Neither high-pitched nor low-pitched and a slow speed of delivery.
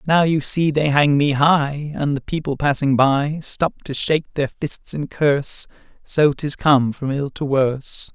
No: medium, 145 Hz; average, 190 wpm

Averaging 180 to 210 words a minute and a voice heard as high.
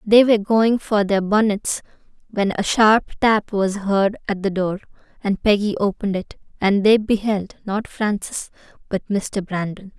No: average, 160 wpm; high, 205 Hz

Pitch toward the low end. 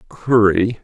Yes: low, 105 Hz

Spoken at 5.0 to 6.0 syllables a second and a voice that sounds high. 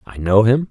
No: 5.1 syllables/s; low, 115 Hz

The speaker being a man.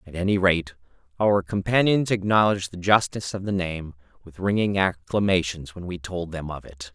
Yes: male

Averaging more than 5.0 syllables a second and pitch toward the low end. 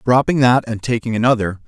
Yes: 5.8 syllables/s; low, 120 Hz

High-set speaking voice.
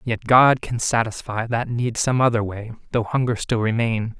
No: low, 115 Hz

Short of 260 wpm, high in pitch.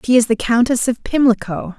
Yes: average, 200 wpm; high, 235 Hz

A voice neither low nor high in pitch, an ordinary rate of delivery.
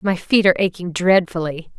Yes: medium, 180 Hz; average, 170 wpm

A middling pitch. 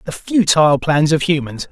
Yes: medium, 160 Hz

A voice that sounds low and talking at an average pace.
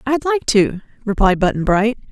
No: high, 225 Hz; average, 170 wpm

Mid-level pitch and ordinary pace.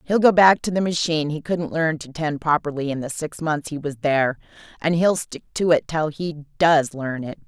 No: medium, 155 Hz; fast, 235 wpm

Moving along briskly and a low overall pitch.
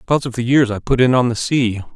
Yes: fast, 305 wpm; low, 120 Hz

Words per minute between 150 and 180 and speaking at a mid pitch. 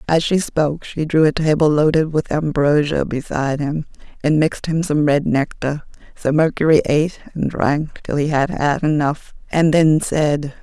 Yes: average, 175 wpm; medium, 150 Hz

